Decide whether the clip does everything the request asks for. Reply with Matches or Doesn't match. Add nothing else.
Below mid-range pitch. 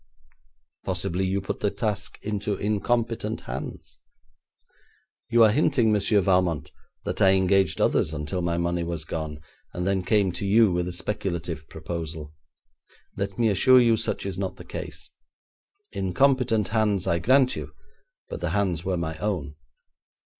Matches